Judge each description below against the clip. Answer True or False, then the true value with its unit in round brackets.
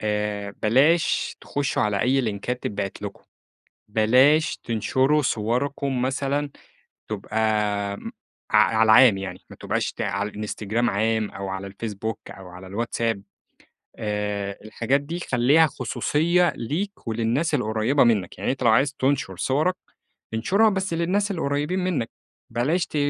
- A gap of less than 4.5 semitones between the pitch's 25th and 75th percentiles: False (5.4 semitones)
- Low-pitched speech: True (115 Hz)